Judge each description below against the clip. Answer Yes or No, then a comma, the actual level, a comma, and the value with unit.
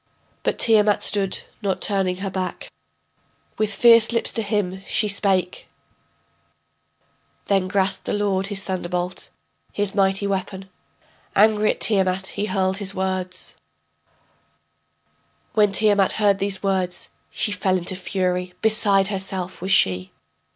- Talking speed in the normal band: No, slow, 125 wpm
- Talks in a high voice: Yes, high, 195 Hz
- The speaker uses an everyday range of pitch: No, narrow, 1.7 semitones